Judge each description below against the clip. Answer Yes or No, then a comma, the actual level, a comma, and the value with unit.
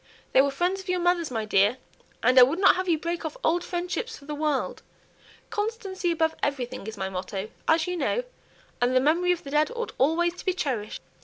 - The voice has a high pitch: Yes, very high, 320 Hz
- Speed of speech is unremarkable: No, fast, 220 wpm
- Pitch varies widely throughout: Yes, wide, 5.7 semitones